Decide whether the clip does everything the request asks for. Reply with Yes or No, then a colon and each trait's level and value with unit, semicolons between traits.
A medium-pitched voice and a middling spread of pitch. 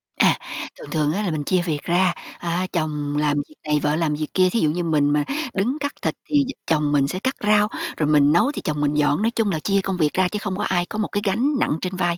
Yes: medium, 170 Hz; average, 4.8 semitones